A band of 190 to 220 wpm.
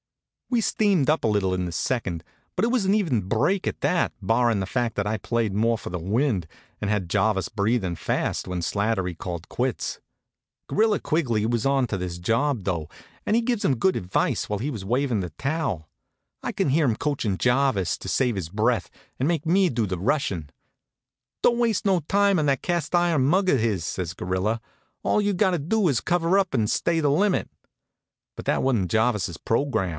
Yes: average, 200 wpm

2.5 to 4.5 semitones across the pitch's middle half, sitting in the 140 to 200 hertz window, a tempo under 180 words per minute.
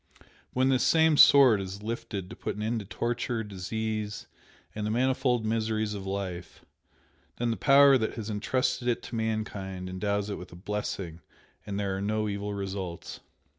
No: average, 3.0 semitones; low, 105 Hz; average, 170 wpm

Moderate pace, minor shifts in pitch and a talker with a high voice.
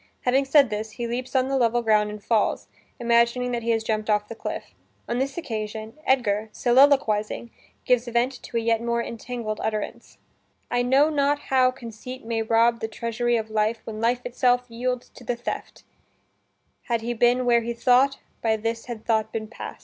Yes: average, 190 wpm; narrow, 2.1 semitones; high, 235 Hz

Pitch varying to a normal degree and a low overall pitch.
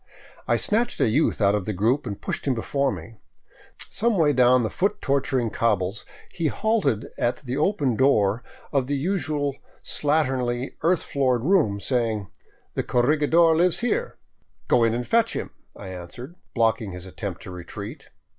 No: wide, 5.9 semitones; low, 130 Hz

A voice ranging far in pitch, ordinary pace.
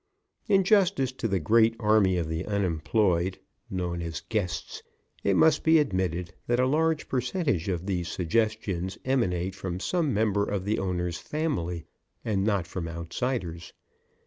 Yes: wide, 5.7 semitones; average, 145 wpm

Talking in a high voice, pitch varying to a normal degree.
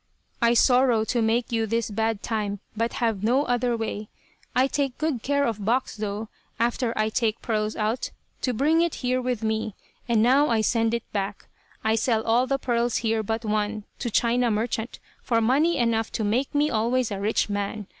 No: high, 230 Hz; narrow, 2.3 semitones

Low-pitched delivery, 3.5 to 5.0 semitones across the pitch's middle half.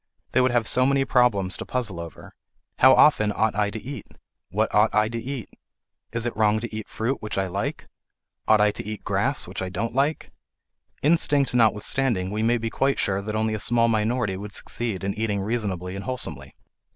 No: low, 110 Hz; average, 3.1 semitones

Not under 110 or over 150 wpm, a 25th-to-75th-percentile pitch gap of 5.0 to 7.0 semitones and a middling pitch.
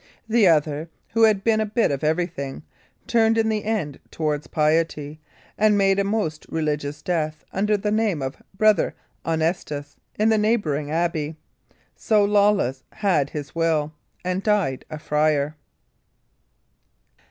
Yes: average, 140 wpm; wide, 5.6 semitones; medium, 165 Hz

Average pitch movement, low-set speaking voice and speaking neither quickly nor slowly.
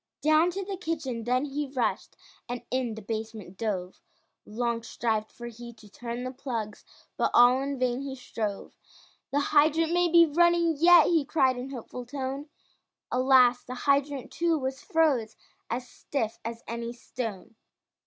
No: average, 4.0 semitones; very high, 255 Hz; average, 160 wpm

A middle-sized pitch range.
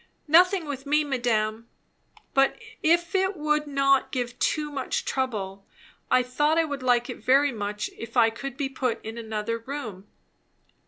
Yes: average, 4.4 semitones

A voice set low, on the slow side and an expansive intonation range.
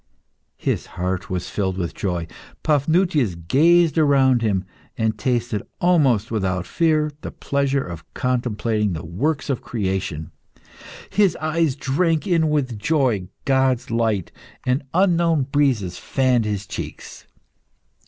Yes: low, 125 Hz; slow, 120 wpm; wide, 6.9 semitones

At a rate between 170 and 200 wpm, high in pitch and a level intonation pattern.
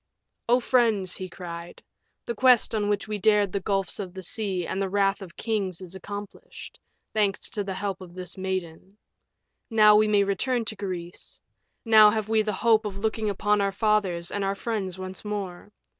Yes: average, 190 wpm; high, 200 Hz; narrow, 2.3 semitones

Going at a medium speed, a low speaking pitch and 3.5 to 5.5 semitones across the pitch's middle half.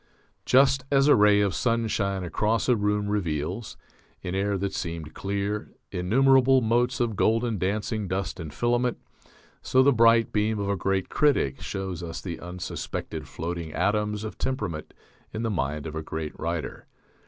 Yes: average, 160 wpm; low, 105 Hz; average, 4.5 semitones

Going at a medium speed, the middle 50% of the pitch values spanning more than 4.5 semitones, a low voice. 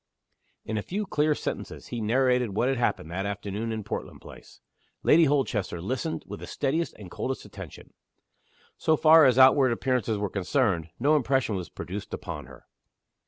Yes: average, 165 wpm; average, 5.2 semitones; low, 125 Hz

